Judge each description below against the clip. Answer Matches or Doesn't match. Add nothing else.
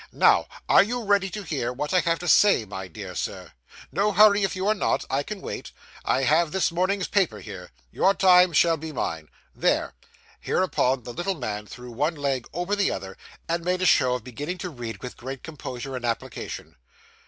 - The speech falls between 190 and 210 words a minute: Matches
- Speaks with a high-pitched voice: Doesn't match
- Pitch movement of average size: Doesn't match